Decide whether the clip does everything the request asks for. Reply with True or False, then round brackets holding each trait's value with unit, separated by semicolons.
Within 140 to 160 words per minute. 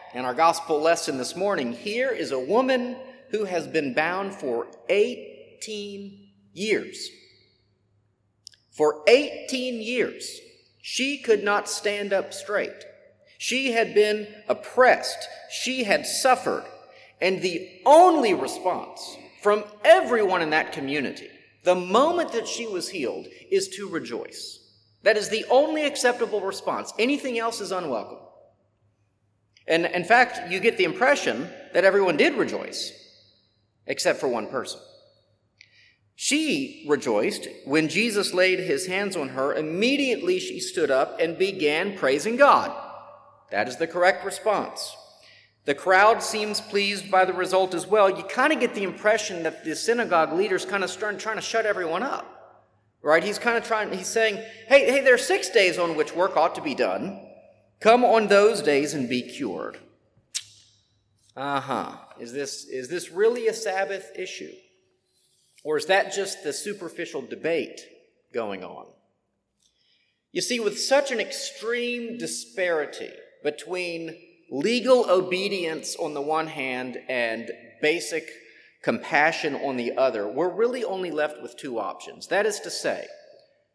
True (145 wpm)